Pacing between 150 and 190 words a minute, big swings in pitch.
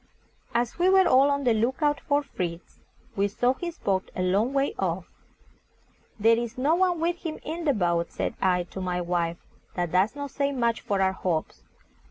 No: average, 200 wpm; wide, 7.7 semitones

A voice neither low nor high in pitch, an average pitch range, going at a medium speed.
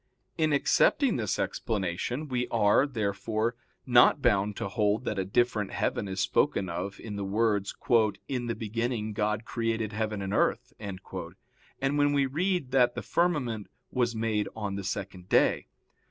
No: low, 110 Hz; average, 3.6 semitones; average, 155 wpm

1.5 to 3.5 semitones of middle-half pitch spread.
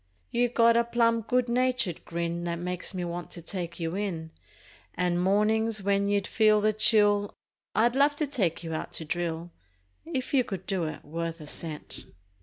No: average, 5.2 semitones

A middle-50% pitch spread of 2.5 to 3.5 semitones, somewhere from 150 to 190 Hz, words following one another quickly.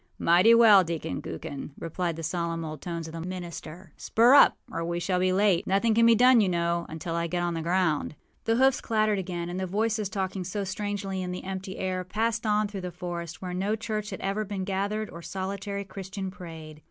Yes: average, 3.2 semitones; medium, 185 Hz; fast, 220 wpm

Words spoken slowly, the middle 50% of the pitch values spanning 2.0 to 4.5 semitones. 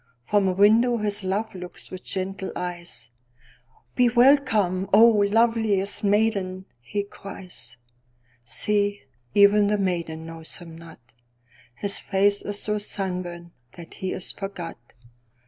Yes: slow, 110 wpm; average, 4.0 semitones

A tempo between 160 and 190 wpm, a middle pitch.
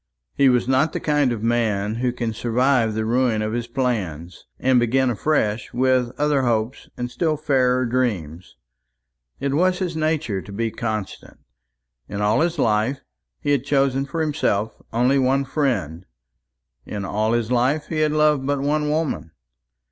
No: average, 165 wpm; low, 125 Hz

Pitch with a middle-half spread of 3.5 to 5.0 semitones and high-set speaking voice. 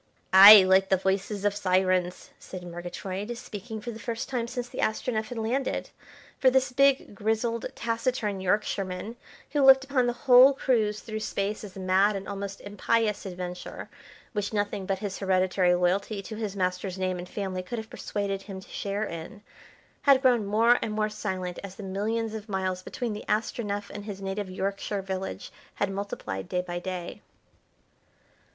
No: average, 3.0 semitones; high, 205 Hz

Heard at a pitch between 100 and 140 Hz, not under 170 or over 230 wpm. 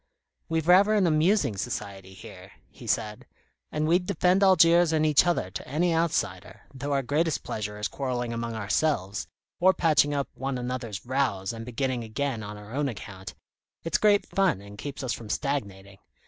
Yes: low, 135 Hz; average, 175 wpm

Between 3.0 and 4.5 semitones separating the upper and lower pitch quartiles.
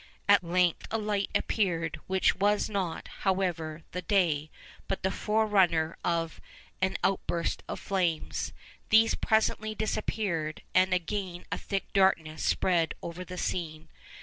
Yes: average, 3.3 semitones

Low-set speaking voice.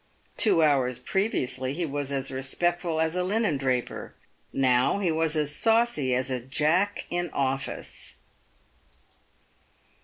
No: medium, 150 Hz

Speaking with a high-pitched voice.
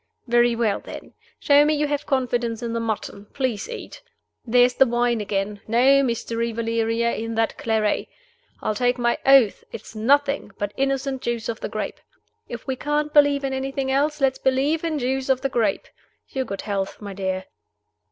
Yes: high, 245 Hz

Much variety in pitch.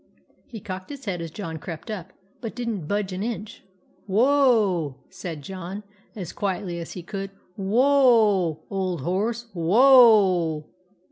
No: average, 4.3 semitones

